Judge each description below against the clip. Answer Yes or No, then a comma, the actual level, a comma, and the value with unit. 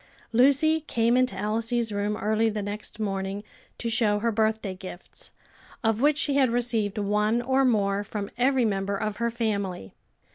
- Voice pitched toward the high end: Yes, high, 220 Hz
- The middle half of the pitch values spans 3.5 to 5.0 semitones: No, average, 2.7 semitones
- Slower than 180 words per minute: Yes, average, 160 wpm